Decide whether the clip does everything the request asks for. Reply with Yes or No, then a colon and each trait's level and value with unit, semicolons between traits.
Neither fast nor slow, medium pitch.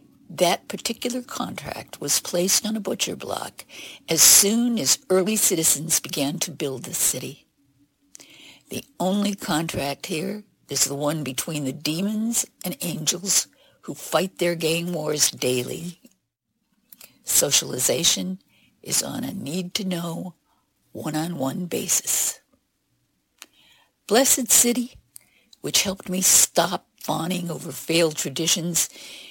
No: slow, 110 wpm; medium, 175 Hz